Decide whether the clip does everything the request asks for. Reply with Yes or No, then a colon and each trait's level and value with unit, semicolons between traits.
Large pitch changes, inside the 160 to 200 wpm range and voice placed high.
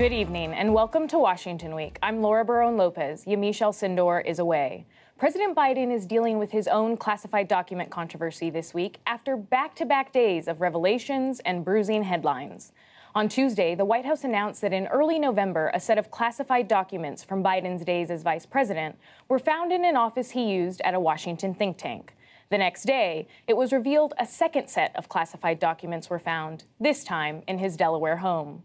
Yes: wide, 6.1 semitones; average, 180 wpm; high, 205 Hz